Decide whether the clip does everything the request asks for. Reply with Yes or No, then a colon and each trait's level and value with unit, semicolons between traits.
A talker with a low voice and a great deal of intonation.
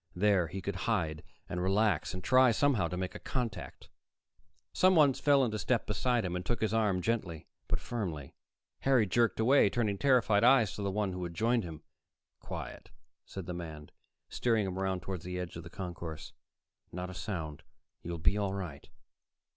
No: very low, 95 Hz; average, 4.4 semitones